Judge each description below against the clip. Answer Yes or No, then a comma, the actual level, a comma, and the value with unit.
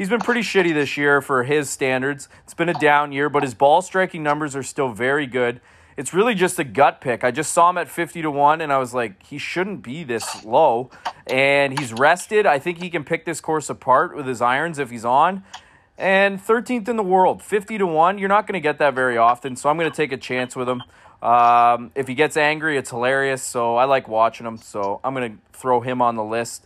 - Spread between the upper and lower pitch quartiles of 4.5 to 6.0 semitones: Yes, average, 5.3 semitones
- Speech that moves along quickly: Yes, fast, 245 wpm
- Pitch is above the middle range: No, medium, 140 Hz